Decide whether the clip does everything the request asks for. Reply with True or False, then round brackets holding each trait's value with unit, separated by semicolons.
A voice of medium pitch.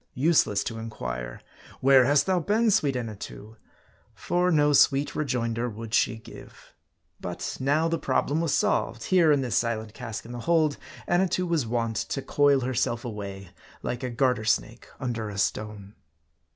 False (125 Hz)